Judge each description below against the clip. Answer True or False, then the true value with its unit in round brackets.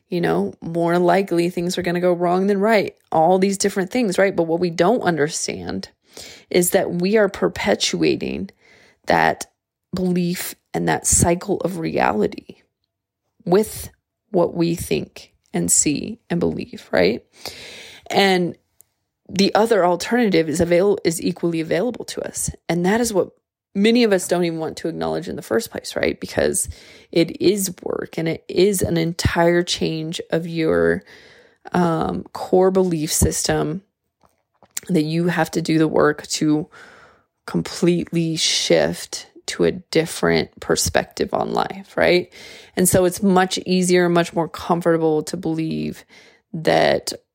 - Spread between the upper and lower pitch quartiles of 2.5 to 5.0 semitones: True (2.8 semitones)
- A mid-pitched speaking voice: True (175 Hz)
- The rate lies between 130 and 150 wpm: True (145 wpm)